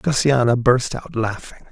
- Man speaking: Yes, male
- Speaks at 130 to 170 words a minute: Yes, average, 140 wpm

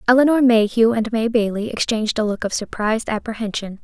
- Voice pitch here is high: Yes, high, 225 Hz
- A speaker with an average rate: Yes, average, 170 wpm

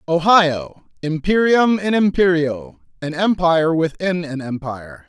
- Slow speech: Yes, slow, 95 wpm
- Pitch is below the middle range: No, medium, 170 Hz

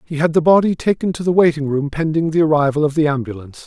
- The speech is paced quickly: Yes, fast, 245 wpm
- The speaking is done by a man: Yes, male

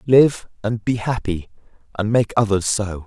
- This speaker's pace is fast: No, average, 155 wpm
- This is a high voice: No, low, 110 Hz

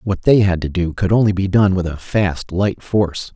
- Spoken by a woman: No, male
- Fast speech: Yes, fast, 250 wpm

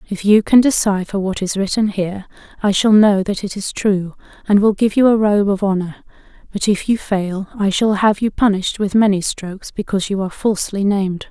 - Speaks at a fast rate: Yes, fast, 210 wpm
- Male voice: No, female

